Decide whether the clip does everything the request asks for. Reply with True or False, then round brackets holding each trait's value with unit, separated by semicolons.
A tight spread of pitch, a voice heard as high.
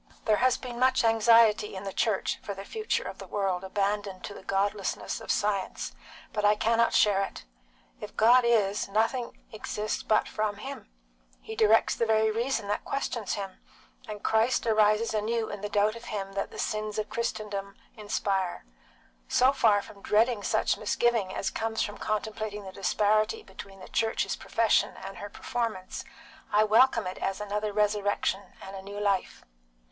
True (2.0 semitones; 210 Hz)